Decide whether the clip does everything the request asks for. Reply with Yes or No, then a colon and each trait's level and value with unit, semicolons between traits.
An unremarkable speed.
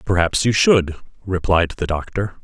Yes: average, 150 wpm